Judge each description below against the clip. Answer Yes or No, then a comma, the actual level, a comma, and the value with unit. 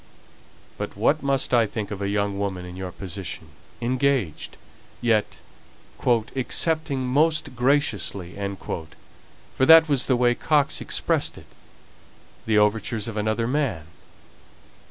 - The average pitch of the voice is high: No, low, 115 Hz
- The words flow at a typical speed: No, slow, 120 wpm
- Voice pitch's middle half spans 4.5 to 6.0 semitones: Yes, average, 5.2 semitones